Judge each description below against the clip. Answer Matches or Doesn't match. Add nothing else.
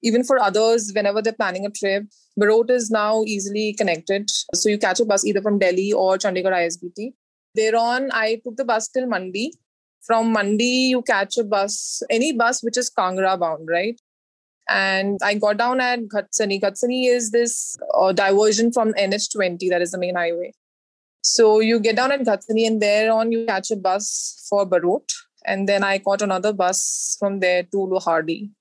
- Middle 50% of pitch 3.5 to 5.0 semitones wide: Doesn't match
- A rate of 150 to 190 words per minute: Matches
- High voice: Matches